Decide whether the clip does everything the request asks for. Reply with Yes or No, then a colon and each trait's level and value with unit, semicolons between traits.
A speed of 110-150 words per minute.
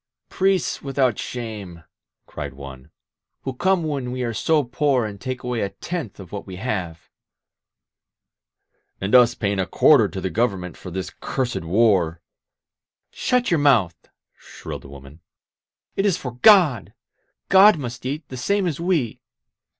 No: average, 160 wpm